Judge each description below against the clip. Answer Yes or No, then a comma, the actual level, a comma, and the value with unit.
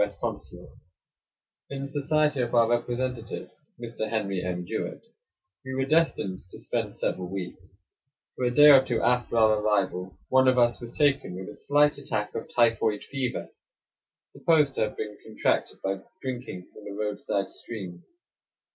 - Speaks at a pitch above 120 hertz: No, low, 115 Hz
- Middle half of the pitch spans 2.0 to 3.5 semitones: No, average, 4.6 semitones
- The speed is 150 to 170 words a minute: Yes, average, 160 wpm